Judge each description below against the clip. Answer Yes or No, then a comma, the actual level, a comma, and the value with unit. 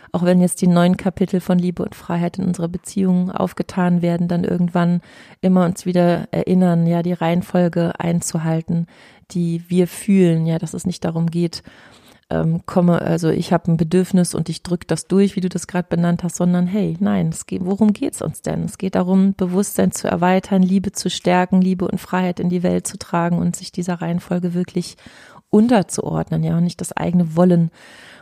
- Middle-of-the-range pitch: Yes, medium, 180 Hz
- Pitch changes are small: Yes, narrow, 1.4 semitones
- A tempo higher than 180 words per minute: Yes, fast, 190 wpm